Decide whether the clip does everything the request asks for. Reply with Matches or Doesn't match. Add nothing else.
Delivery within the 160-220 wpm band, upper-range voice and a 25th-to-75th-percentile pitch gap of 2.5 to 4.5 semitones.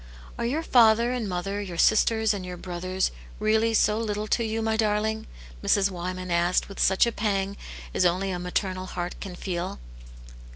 Matches